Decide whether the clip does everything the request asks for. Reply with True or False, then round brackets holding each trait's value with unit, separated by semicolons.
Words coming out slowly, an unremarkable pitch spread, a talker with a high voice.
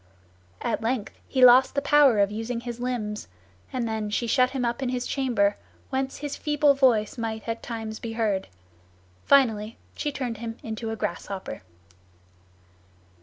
False (160 wpm; 3.0 semitones; 235 Hz)